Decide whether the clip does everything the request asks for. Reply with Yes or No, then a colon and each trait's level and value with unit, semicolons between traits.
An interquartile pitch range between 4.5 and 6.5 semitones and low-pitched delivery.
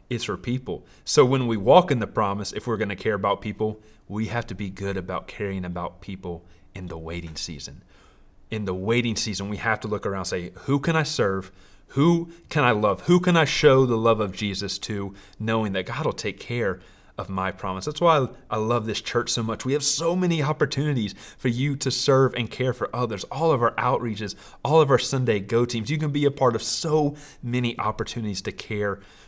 Yes: average, 4.8 semitones; low, 110 Hz